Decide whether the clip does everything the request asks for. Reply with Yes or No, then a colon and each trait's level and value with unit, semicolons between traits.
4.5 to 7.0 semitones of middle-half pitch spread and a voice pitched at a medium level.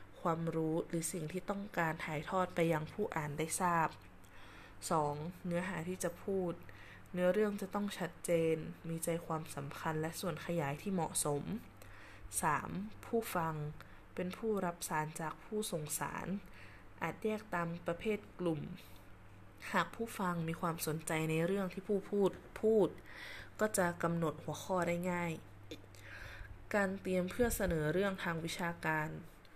No: average, 3.1 semitones; medium, 170 Hz